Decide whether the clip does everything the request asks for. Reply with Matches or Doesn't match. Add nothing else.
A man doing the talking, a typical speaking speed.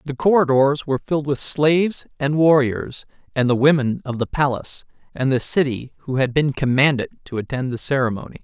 Matches